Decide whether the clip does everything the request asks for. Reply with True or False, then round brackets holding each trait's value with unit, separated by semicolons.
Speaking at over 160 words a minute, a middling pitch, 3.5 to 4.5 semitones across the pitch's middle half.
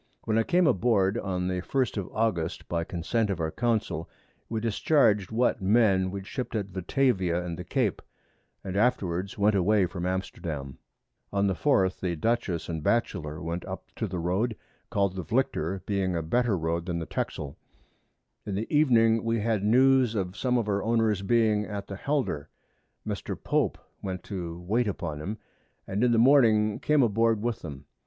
False (175 wpm; 100 Hz; 4.2 semitones)